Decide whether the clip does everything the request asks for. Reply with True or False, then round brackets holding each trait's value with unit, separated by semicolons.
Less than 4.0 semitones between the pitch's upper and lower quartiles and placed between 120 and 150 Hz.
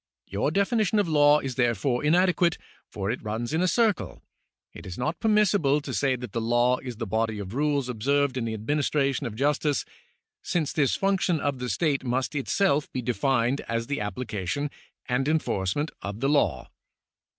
False (4.4 semitones; 135 Hz)